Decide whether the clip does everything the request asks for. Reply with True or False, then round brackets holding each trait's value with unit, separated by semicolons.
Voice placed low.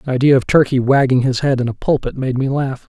True (130 Hz)